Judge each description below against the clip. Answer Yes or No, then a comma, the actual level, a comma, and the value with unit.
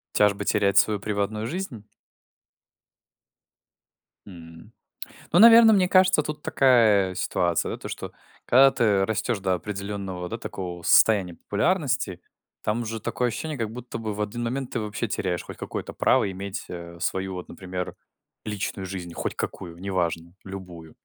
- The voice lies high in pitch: No, low, 100 Hz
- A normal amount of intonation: Yes, average, 4.2 semitones